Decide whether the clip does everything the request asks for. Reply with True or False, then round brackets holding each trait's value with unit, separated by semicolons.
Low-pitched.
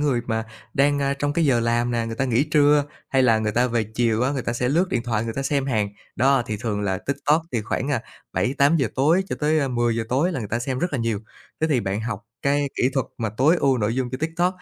True (130 Hz)